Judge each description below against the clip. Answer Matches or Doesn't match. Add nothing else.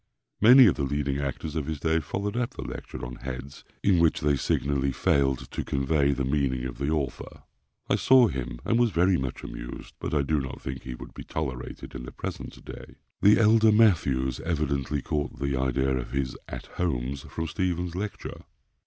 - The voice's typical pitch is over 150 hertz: Doesn't match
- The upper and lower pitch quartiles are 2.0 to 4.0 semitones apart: Doesn't match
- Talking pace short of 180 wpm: Doesn't match